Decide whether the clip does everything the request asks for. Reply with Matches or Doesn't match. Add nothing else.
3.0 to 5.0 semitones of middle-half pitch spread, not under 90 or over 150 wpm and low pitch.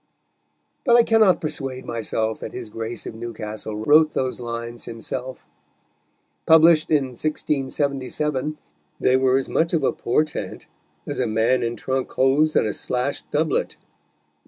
Matches